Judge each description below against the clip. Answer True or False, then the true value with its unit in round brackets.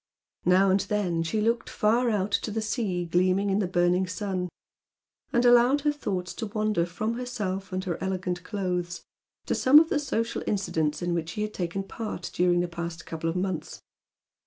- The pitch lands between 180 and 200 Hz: True (190 Hz)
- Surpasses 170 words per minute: True (185 wpm)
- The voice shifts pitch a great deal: False (3.4 semitones)